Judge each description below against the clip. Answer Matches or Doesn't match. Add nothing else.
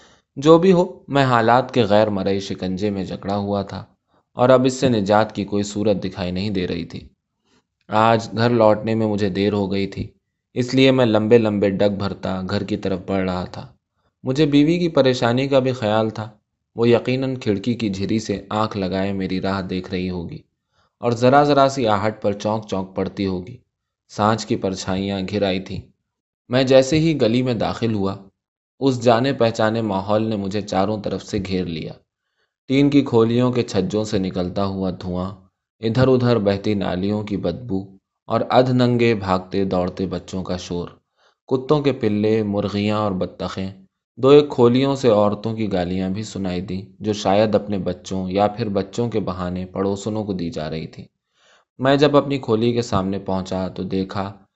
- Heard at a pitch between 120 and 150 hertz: Doesn't match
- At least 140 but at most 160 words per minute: Doesn't match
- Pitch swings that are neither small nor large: Matches